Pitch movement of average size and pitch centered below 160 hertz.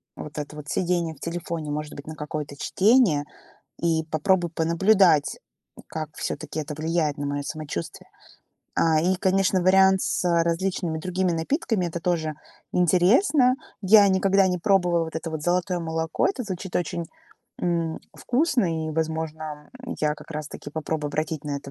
No: average, 3.2 semitones; medium, 165 Hz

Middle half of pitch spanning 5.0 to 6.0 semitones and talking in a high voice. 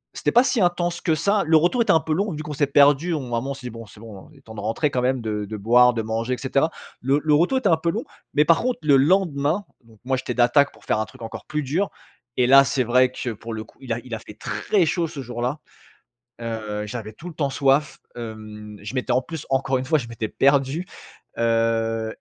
No: average, 5.3 semitones; low, 130 Hz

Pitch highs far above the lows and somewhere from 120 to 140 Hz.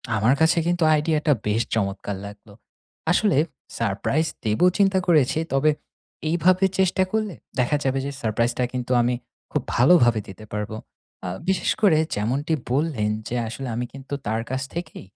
Yes: wide, 6.7 semitones; low, 135 Hz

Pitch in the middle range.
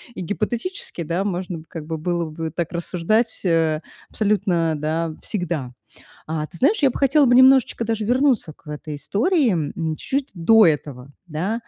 Yes: medium, 175 Hz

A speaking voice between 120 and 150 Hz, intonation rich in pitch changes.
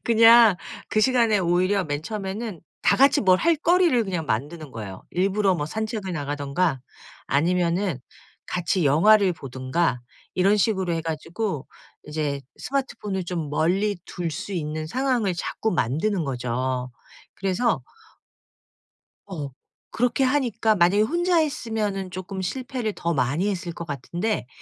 No: medium, 185 Hz; wide, 5.7 semitones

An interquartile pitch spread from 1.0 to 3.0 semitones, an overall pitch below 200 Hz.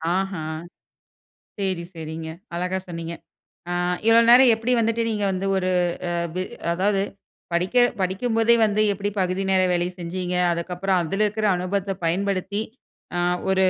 Yes: narrow, 2.5 semitones; high, 190 Hz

